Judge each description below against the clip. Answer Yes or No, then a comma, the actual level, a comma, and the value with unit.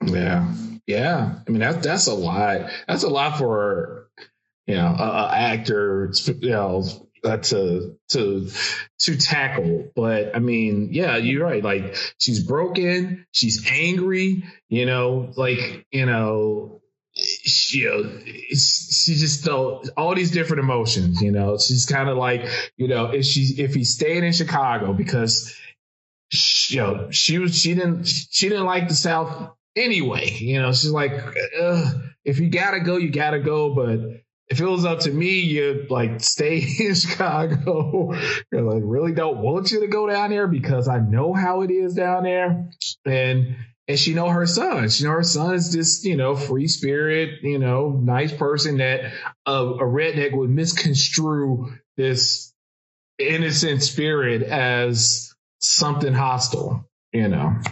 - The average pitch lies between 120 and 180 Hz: Yes, medium, 140 Hz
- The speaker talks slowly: No, average, 155 wpm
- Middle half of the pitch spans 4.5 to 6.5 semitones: Yes, average, 5.3 semitones